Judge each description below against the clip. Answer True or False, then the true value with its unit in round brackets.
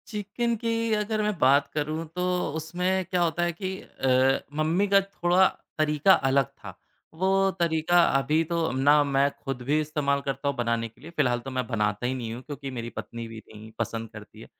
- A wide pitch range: True (5.7 semitones)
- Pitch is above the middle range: False (150 Hz)